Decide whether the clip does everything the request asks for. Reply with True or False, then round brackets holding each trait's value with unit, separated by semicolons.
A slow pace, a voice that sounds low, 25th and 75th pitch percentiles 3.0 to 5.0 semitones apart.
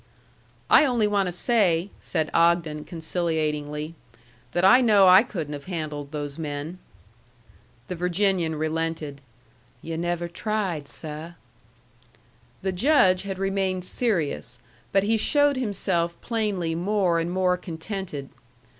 False (120 wpm; 175 Hz; 3.6 semitones)